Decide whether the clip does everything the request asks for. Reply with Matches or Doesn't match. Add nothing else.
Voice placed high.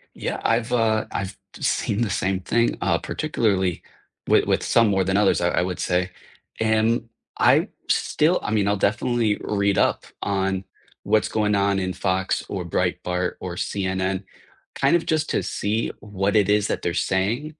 Doesn't match